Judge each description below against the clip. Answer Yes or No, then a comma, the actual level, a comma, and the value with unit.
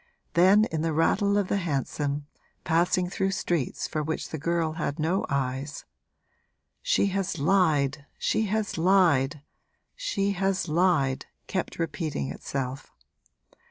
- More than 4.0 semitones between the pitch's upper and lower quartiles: Yes, average, 4.9 semitones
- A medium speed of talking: No, slow, 125 wpm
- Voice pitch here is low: No, medium, 165 Hz